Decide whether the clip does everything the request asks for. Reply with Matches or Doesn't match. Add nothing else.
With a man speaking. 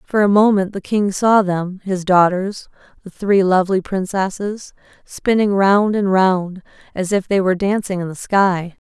Doesn't match